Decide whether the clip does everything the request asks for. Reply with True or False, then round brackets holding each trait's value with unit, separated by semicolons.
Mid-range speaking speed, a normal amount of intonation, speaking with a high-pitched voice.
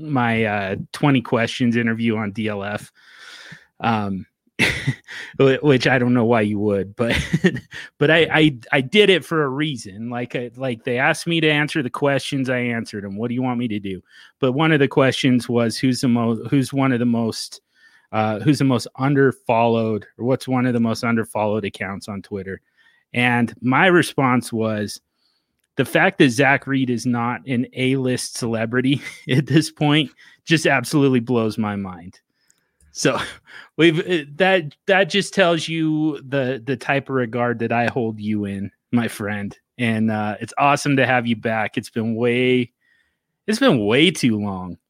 False (175 wpm; 3.9 semitones; 125 Hz)